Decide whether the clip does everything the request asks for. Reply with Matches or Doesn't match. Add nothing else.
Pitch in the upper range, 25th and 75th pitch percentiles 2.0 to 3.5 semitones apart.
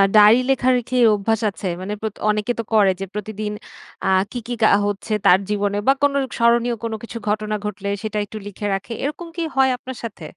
Matches